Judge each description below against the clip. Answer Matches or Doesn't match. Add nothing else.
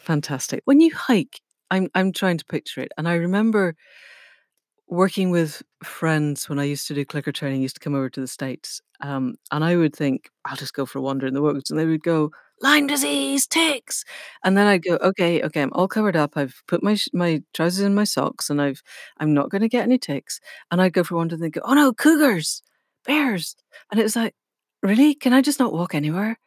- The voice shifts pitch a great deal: Matches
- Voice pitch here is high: Doesn't match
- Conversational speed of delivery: Doesn't match